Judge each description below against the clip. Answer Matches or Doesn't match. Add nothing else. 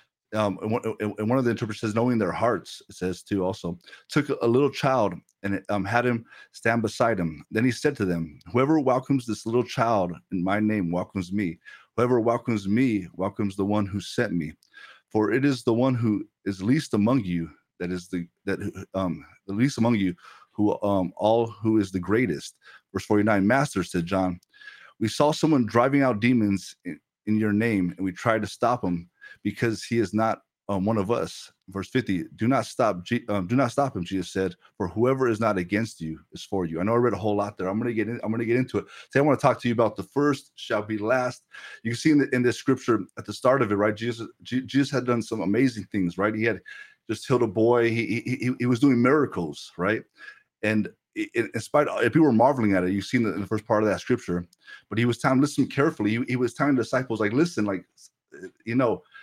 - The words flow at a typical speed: Doesn't match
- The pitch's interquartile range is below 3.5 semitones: Doesn't match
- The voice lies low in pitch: Matches